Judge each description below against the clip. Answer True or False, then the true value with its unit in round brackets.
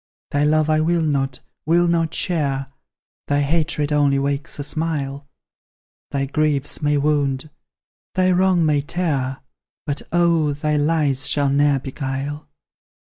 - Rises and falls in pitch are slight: True (2.3 semitones)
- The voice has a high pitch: False (145 Hz)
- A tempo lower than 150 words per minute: True (135 wpm)